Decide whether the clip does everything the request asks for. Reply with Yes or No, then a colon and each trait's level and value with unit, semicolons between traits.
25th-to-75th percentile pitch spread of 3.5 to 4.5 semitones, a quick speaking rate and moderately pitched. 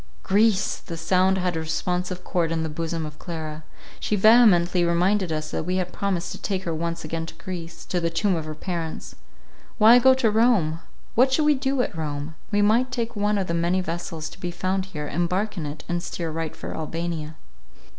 Yes: average, 3.8 semitones; fast, 210 wpm; medium, 175 Hz